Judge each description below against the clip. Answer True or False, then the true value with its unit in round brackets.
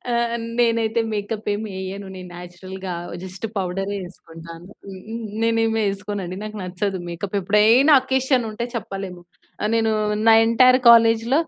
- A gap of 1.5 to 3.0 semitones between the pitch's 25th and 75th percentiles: False (3.5 semitones)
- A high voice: True (205 Hz)